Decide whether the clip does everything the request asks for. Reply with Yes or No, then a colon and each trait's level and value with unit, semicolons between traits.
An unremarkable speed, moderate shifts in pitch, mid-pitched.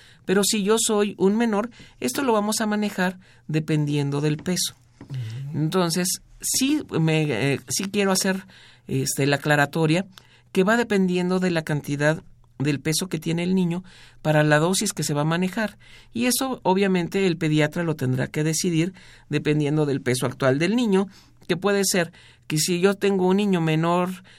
Yes: average, 170 wpm; average, 4.6 semitones; medium, 170 Hz